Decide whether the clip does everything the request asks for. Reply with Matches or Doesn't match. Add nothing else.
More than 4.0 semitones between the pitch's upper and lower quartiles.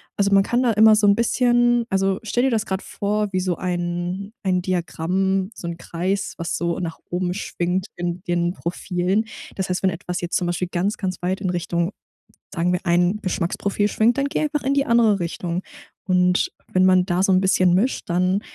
Doesn't match